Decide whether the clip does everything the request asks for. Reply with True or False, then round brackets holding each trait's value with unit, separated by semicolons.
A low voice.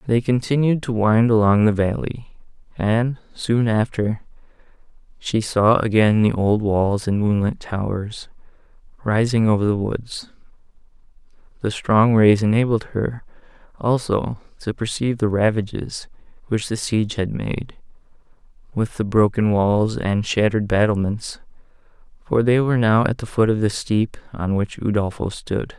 True (110 Hz)